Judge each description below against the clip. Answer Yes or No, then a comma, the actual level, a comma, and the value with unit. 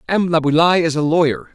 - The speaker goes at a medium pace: Yes, average, 195 wpm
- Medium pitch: Yes, medium, 165 Hz